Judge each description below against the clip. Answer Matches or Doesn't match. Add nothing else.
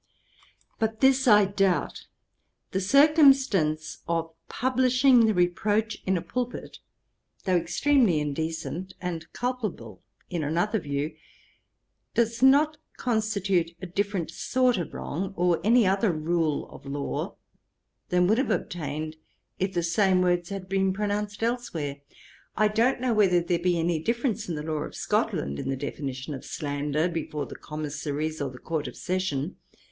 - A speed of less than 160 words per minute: Matches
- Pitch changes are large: Matches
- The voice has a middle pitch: Matches